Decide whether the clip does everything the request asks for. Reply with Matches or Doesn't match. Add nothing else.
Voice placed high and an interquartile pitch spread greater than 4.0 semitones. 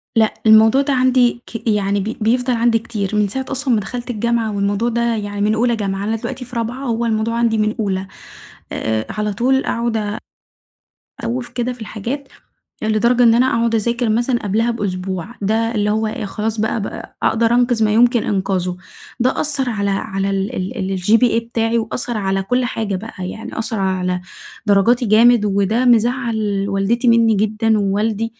Doesn't match